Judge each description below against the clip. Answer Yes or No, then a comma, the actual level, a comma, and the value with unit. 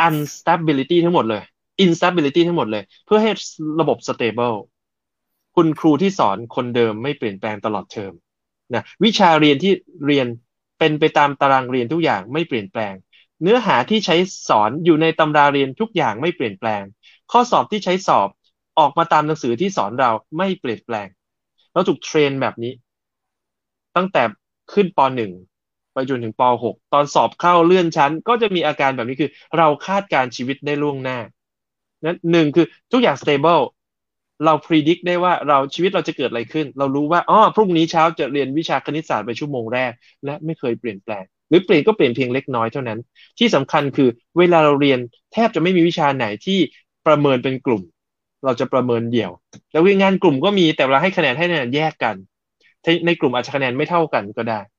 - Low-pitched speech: No, medium, 150 Hz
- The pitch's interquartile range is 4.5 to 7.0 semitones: Yes, average, 5.2 semitones